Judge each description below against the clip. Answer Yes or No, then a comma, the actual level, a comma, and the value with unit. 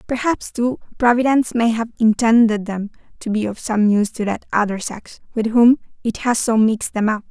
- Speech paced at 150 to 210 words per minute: Yes, average, 195 wpm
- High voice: Yes, high, 225 Hz